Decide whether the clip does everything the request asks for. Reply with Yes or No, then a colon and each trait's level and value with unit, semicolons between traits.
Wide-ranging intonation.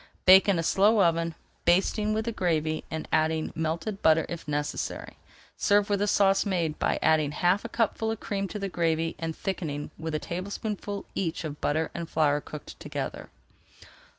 No: average, 4.0 semitones